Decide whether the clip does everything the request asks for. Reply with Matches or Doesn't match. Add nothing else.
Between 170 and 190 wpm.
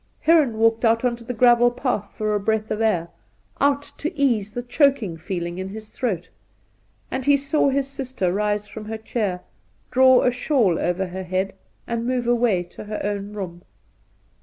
Matches